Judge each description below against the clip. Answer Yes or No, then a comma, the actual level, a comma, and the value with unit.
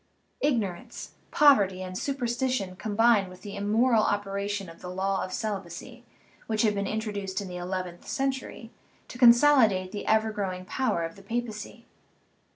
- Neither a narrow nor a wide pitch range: Yes, average, 3.8 semitones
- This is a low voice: No, high, 205 Hz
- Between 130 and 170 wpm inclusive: Yes, average, 160 wpm